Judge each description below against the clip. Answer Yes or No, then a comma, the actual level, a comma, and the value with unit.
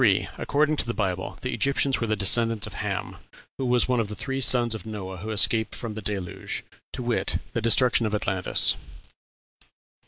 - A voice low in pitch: Yes, low, 115 Hz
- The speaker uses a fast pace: No, average, 180 wpm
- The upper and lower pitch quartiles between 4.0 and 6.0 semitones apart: No, average, 3.1 semitones